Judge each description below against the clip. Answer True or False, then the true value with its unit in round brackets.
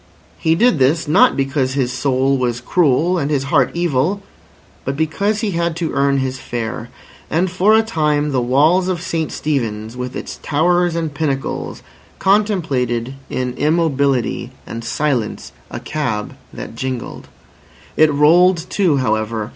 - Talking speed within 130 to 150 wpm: True (145 wpm)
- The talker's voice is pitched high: False (145 Hz)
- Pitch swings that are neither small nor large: True (4.9 semitones)